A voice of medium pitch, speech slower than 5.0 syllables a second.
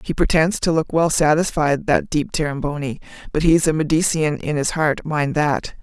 Yes: medium, 155 Hz; 4.8 syllables/s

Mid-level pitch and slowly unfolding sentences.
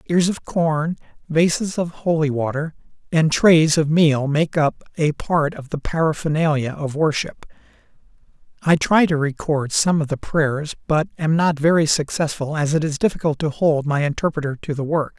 No: medium, 155 Hz; average, 175 wpm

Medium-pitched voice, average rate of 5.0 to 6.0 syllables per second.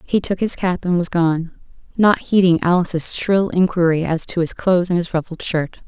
Yes: medium, 175 Hz; 5.1 syllables/s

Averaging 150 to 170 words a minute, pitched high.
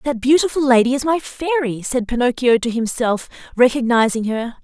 Yes: average, 155 wpm; very high, 250 Hz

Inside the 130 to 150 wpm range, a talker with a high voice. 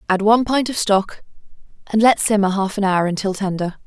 No: average, 200 wpm; high, 205 Hz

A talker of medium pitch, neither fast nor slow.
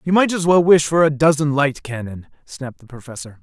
No: medium, 145 Hz; fast, 225 wpm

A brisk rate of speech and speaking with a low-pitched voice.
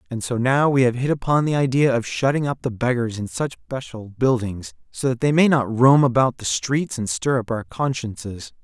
Yes: fast, 220 wpm; low, 125 Hz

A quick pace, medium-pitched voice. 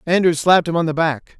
Yes: fast, 260 wpm; medium, 165 Hz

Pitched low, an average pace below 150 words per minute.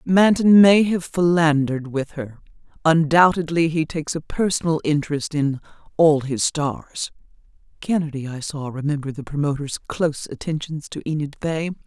No: medium, 155 Hz; slow, 135 wpm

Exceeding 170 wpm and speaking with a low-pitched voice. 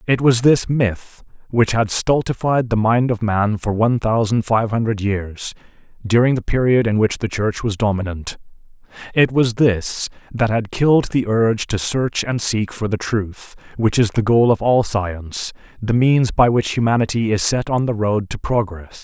Yes: average, 190 wpm; low, 110 Hz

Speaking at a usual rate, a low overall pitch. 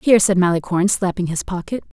No: average, 180 wpm; medium, 185 Hz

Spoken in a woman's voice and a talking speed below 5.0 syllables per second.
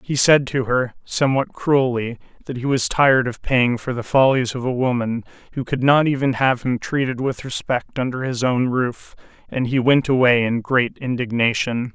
No: male; 4.8 syllables/s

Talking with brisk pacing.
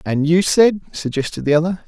No: average, 190 wpm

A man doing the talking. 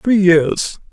Yes: male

